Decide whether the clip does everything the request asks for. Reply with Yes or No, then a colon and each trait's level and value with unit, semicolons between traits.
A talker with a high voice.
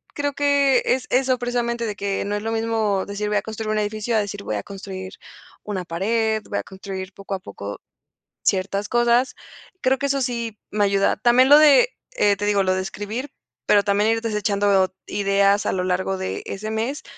Yes: high, 210 Hz